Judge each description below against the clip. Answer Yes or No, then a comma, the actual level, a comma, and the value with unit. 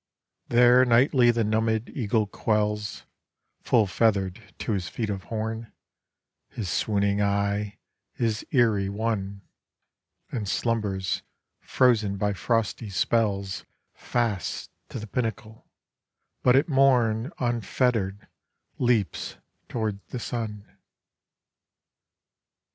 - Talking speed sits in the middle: No, slow, 100 wpm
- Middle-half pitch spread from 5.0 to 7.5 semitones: No, narrow, 2.6 semitones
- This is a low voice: Yes, low, 110 Hz